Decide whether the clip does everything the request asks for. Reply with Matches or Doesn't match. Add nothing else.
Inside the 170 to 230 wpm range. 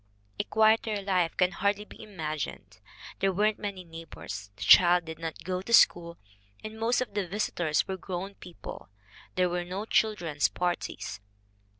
Doesn't match